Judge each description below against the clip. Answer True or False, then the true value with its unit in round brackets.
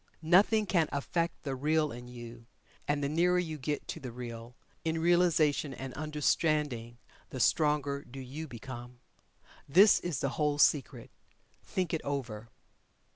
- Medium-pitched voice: True (145 Hz)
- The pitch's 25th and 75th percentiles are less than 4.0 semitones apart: False (4.3 semitones)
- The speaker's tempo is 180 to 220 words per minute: False (145 wpm)